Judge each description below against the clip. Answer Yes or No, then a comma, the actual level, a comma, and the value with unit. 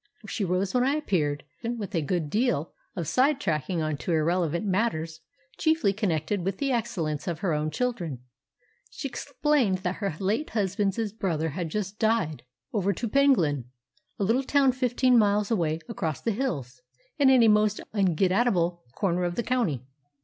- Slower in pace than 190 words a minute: Yes, average, 180 wpm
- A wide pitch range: Yes, wide, 6.1 semitones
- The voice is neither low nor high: No, high, 195 Hz